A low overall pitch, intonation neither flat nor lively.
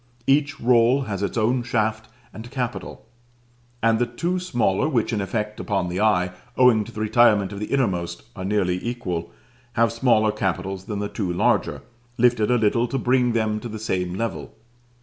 Yes: low, 110 Hz; average, 3.3 semitones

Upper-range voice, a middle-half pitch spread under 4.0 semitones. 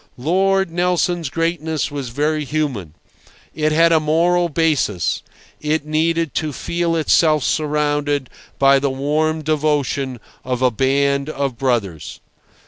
No: medium, 150 Hz; average, 2.9 semitones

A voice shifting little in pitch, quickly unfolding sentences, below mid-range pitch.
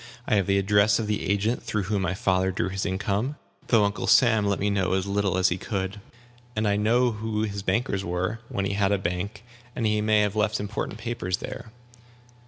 Yes: narrow, 2.0 semitones; fast, 215 wpm; low, 100 Hz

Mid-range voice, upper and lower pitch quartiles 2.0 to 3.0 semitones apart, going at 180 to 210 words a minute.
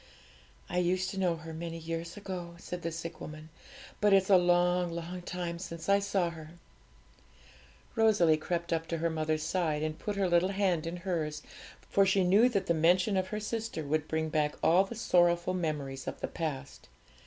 Yes: medium, 175 Hz; narrow, 2.6 semitones; average, 190 wpm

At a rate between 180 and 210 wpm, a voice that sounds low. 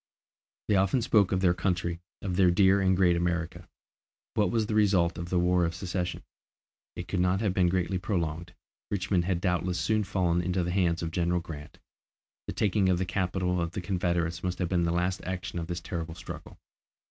Yes: average, 200 wpm; very low, 90 Hz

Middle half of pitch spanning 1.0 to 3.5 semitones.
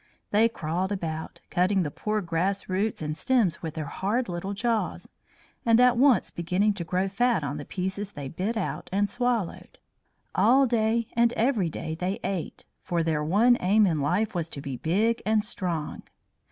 No: average, 5.0 semitones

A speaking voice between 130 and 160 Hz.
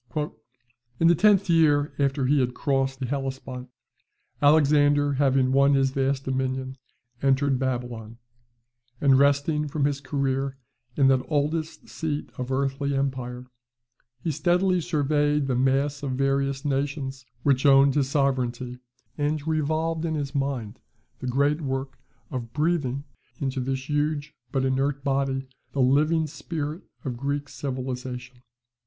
Yes: medium, 140 Hz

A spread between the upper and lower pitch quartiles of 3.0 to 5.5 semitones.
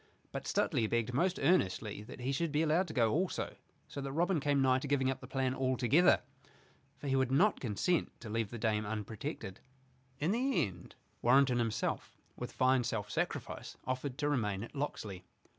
Yes: average, 4.4 semitones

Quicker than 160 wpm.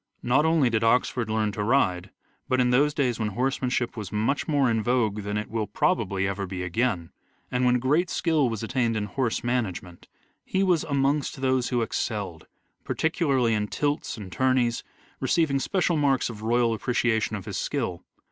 Yes: average, 180 wpm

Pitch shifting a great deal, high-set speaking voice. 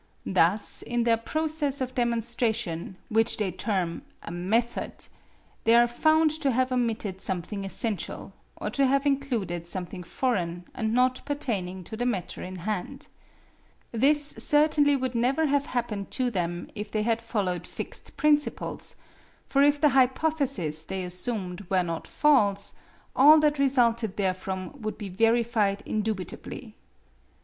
Yes: wide, 5.8 semitones; high, 230 Hz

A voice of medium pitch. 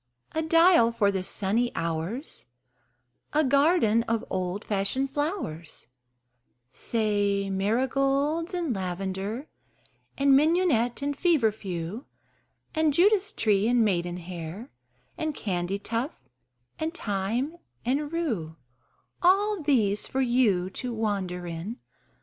No: high, 230 Hz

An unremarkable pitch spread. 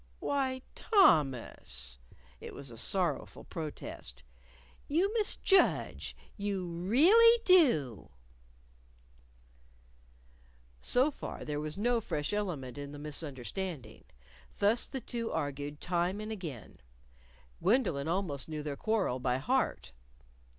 No: wide, 8.6 semitones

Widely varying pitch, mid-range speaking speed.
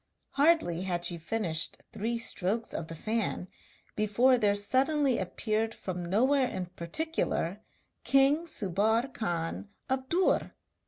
No: wide, 6.4 semitones; slow, 120 wpm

